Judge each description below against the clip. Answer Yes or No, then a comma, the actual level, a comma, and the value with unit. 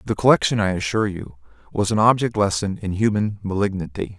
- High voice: No, low, 100 Hz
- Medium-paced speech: Yes, average, 170 wpm